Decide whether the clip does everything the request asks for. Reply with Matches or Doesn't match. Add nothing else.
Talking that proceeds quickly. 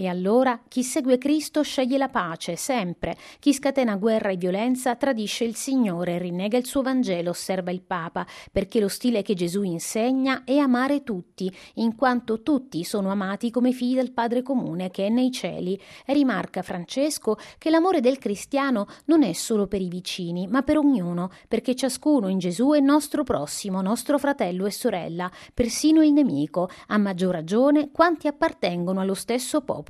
Matches